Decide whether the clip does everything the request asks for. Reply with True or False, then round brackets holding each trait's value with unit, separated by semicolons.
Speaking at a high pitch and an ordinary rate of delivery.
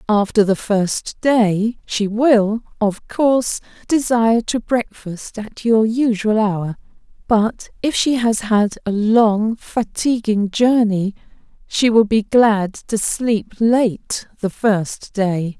False (220 Hz; 130 wpm)